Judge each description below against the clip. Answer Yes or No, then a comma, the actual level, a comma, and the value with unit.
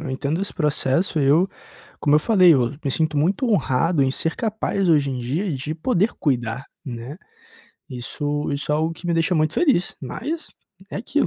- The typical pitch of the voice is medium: Yes, medium, 155 Hz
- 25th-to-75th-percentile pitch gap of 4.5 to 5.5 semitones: Yes, average, 4.9 semitones